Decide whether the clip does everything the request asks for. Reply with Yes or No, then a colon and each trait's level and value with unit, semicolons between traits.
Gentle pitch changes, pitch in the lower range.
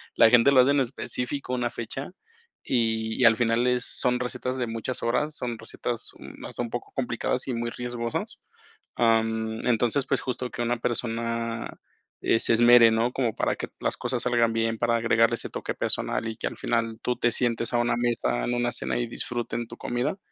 Yes: narrow, 1.3 semitones; low, 120 Hz